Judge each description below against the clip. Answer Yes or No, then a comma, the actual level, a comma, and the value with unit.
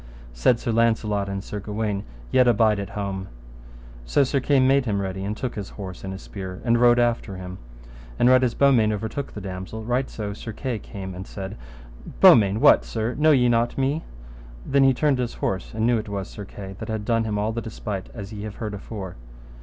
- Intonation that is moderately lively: Yes, average, 3.4 semitones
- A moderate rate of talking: No, fast, 215 wpm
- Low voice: Yes, low, 110 Hz